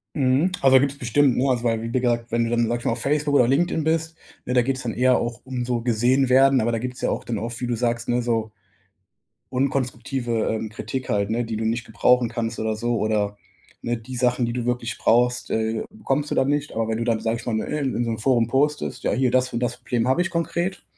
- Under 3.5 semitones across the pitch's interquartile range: Yes, narrow, 2.4 semitones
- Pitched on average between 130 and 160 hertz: No, low, 120 Hz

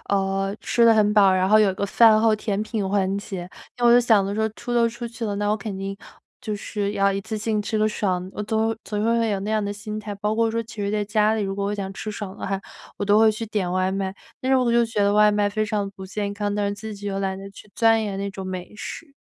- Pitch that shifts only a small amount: Yes, narrow, 1.8 semitones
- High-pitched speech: Yes, high, 210 Hz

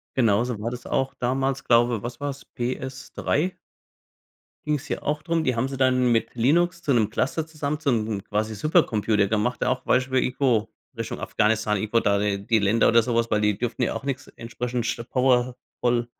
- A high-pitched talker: No, low, 120 Hz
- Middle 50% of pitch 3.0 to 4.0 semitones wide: Yes, average, 3.3 semitones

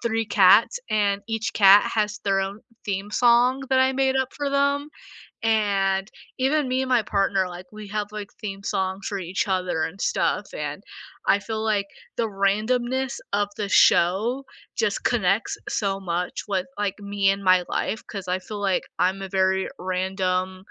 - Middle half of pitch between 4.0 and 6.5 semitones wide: No, average, 2.8 semitones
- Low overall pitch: No, high, 200 Hz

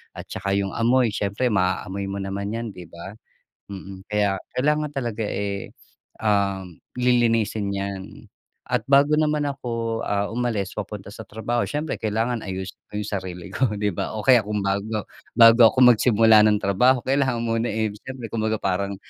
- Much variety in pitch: No, average, 3.3 semitones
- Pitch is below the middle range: Yes, low, 110 Hz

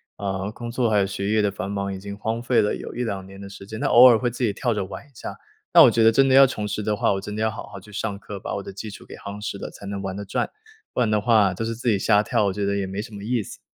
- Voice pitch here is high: No, low, 105 Hz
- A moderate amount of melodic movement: No, narrow, 2.3 semitones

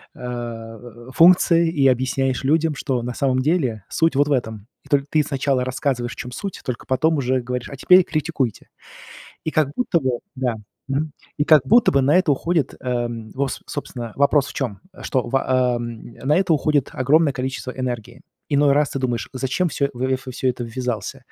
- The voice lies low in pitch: Yes, low, 130 Hz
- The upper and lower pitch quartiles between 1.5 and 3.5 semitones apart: Yes, average, 3.2 semitones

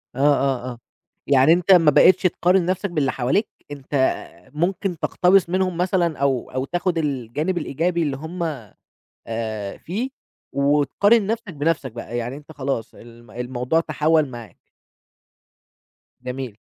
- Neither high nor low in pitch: Yes, medium, 150 Hz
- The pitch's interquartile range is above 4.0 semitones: Yes, wide, 5.4 semitones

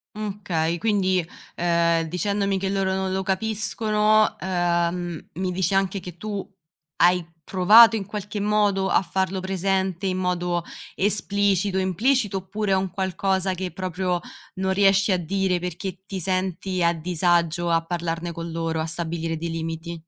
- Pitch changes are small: Yes, narrow, 2.2 semitones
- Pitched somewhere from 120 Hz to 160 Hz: No, medium, 185 Hz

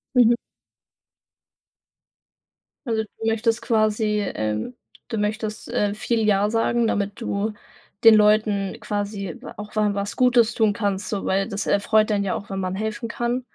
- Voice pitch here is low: No, high, 210 Hz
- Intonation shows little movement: Yes, narrow, 1.9 semitones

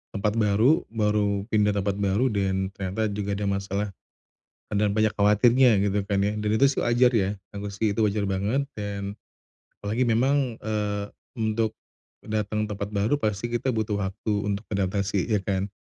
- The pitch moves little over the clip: Yes, narrow, 1.5 semitones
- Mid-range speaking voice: No, low, 105 Hz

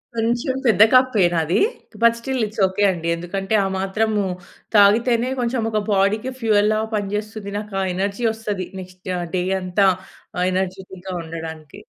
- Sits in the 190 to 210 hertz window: Yes, high, 205 Hz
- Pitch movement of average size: Yes, average, 3.1 semitones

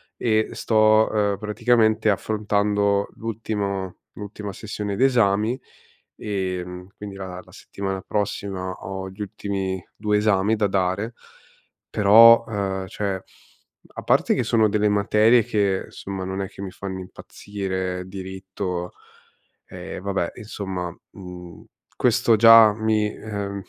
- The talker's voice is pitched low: Yes, low, 100 Hz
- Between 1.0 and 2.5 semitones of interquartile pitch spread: Yes, narrow, 2.1 semitones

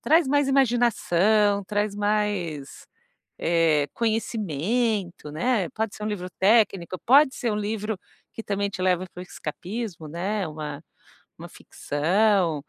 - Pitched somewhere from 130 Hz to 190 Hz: No, high, 205 Hz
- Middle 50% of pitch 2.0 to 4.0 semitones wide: No, average, 4.4 semitones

